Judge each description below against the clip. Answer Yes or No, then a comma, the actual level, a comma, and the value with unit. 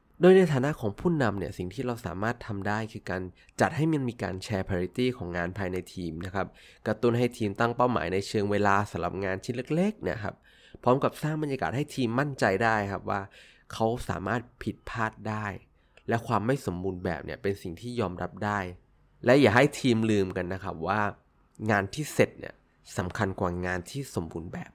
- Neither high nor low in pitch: No, low, 105 Hz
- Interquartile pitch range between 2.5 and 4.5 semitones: No, average, 4.9 semitones